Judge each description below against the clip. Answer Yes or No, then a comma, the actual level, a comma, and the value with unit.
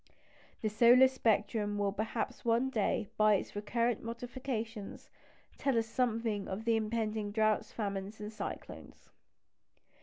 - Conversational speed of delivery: No, slow, 120 wpm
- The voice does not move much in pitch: Yes, narrow, 1.9 semitones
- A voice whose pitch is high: Yes, high, 220 Hz